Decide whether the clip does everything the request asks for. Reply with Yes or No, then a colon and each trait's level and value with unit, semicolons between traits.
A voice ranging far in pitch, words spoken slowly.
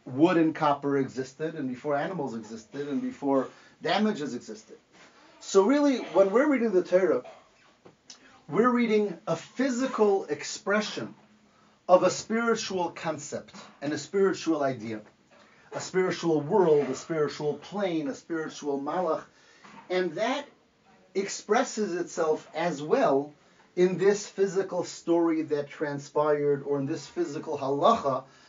Yes: wide, 5.7 semitones; slow, 120 wpm